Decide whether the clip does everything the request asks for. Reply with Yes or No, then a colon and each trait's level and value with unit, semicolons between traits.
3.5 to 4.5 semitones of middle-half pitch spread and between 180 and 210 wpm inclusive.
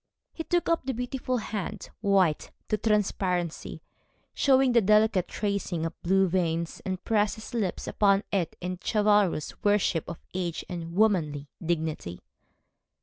No: average, 3.9 semitones; average, 140 wpm